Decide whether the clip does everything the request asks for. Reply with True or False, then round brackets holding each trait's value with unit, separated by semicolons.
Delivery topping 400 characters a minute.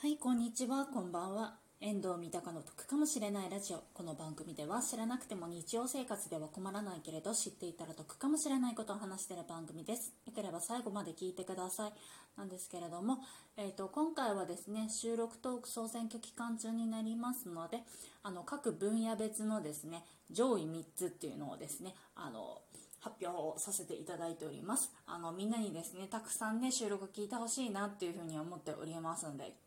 True (425 characters per minute)